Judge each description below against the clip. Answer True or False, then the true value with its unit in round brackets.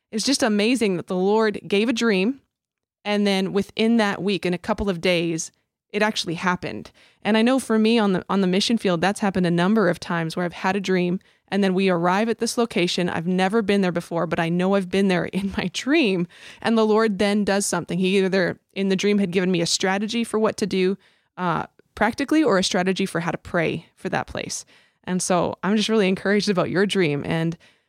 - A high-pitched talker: True (195 Hz)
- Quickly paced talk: True (230 wpm)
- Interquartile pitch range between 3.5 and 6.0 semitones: False (3.0 semitones)